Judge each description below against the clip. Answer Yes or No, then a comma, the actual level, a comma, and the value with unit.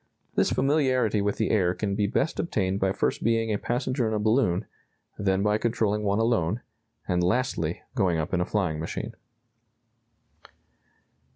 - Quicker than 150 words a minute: Yes, average, 160 wpm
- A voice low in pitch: Yes, low, 105 Hz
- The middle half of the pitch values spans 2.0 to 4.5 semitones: Yes, average, 3.5 semitones